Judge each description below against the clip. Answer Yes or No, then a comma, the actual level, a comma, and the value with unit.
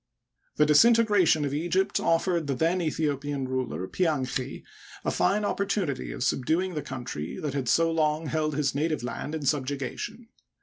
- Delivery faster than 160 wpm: Yes, average, 170 wpm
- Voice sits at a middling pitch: Yes, medium, 150 Hz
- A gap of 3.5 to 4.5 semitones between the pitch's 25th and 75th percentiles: Yes, average, 3.8 semitones